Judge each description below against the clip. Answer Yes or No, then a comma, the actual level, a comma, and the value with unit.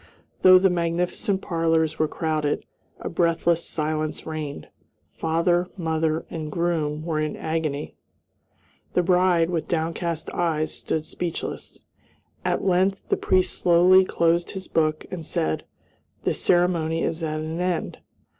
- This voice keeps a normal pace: No, slow, 130 wpm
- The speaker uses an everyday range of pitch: No, narrow, 2.0 semitones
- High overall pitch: No, medium, 165 Hz